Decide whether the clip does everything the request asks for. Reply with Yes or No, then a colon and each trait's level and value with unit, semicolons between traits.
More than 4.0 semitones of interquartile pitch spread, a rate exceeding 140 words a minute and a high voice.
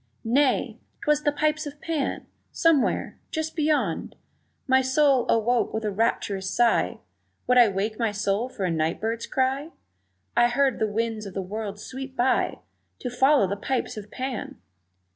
Yes: average, 4.4 semitones; average, 160 wpm; high, 240 Hz